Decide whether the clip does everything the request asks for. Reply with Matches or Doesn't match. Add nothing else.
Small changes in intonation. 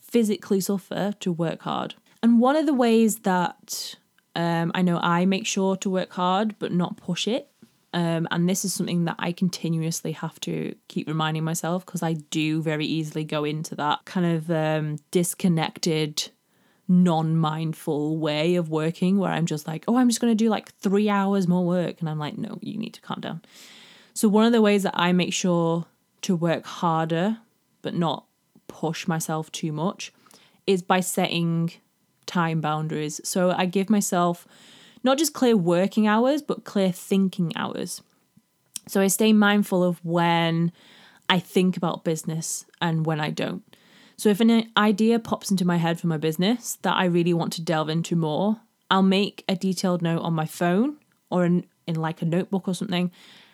Doesn't match